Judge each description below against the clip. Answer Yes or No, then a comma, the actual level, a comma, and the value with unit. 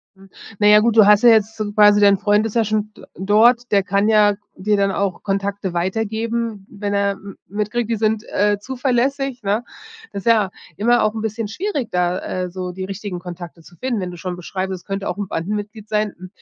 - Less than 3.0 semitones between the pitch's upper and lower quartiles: Yes, narrow, 2.4 semitones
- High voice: Yes, high, 205 Hz